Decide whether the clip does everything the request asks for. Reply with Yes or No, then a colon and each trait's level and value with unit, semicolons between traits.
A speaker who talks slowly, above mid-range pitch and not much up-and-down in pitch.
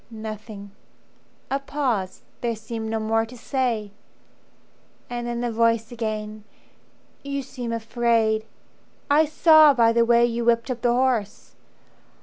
Yes: slow, 130 wpm; high, 230 Hz; narrow, 2.0 semitones